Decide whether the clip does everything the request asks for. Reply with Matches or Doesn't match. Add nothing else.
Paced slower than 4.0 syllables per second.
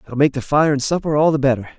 Doesn't match